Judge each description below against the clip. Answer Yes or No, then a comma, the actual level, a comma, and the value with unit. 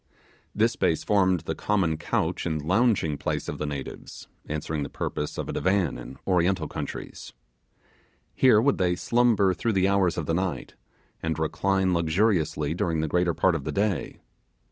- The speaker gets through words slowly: No, average, 165 wpm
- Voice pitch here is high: No, very low, 90 Hz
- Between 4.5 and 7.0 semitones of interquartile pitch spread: No, average, 3.7 semitones